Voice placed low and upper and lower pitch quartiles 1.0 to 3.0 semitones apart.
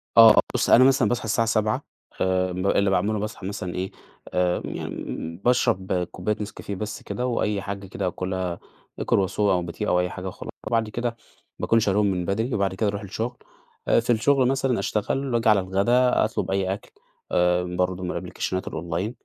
No: low, 100 Hz; average, 3.5 semitones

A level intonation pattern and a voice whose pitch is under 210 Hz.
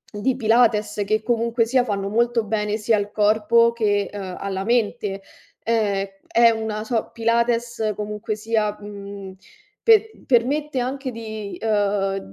No: narrow, 2.3 semitones; high, 220 Hz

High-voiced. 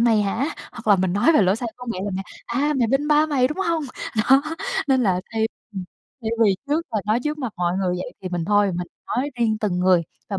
Yes: high, 220 Hz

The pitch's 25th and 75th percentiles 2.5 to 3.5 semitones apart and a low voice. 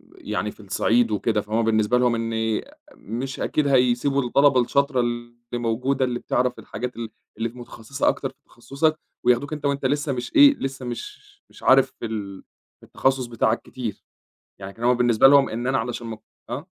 Yes: average, 2.9 semitones; low, 120 Hz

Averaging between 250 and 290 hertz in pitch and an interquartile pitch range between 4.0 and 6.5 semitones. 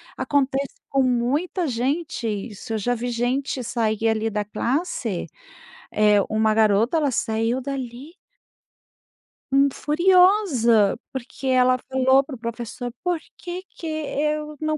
Yes: very high, 255 Hz; average, 4.5 semitones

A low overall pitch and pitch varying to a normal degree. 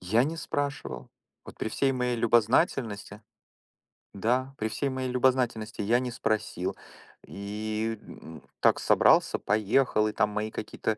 Yes: low, 110 Hz; average, 3.2 semitones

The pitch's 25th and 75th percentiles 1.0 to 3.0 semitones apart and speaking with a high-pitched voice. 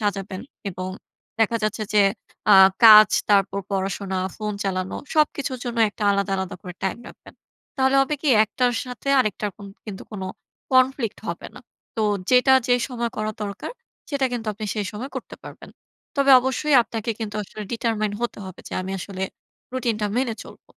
No: average, 4.0 semitones; high, 215 Hz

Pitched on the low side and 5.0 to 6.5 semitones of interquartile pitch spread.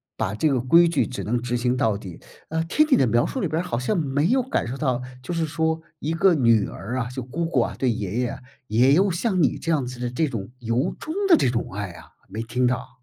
Yes: low, 130 Hz; wide, 5.6 semitones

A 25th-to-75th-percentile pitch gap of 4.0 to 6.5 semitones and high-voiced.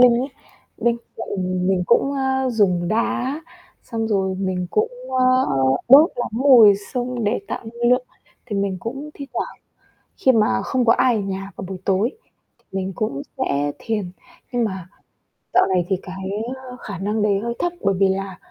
Yes: average, 4.6 semitones; high, 215 Hz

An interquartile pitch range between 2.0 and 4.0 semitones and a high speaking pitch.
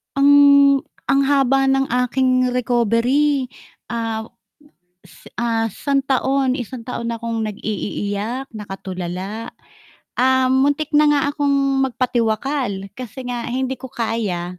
Yes: average, 3.3 semitones; very high, 250 Hz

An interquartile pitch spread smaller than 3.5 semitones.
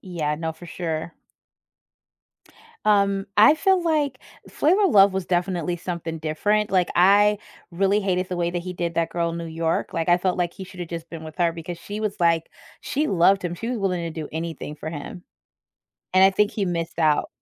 Yes: average, 3.0 semitones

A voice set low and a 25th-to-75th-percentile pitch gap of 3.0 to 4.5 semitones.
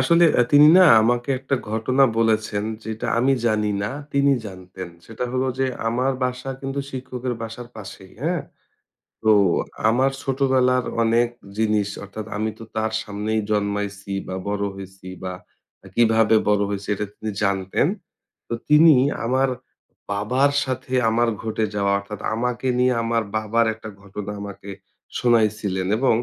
Yes: low, 110 Hz; average, 3.8 semitones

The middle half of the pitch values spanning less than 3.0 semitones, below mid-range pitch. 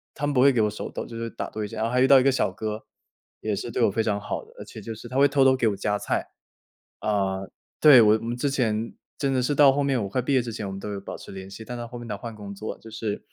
No: average, 3.5 semitones; low, 115 Hz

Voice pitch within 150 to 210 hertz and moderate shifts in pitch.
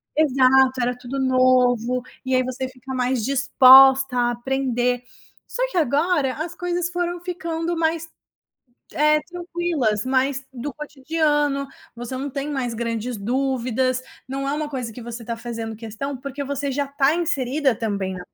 No: very high, 265 Hz; average, 3.0 semitones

